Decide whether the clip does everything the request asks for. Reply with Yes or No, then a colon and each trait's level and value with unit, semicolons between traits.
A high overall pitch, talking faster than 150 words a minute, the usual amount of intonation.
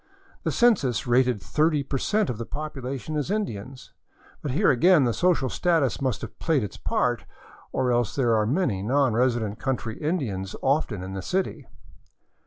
No: low, 130 Hz; average, 160 wpm; average, 4.7 semitones